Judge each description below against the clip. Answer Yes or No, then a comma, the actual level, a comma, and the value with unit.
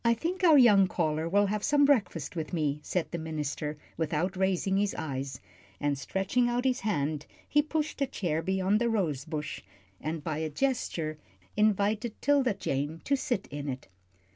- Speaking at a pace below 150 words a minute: No, average, 175 wpm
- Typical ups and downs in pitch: No, wide, 7.3 semitones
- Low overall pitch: No, medium, 185 Hz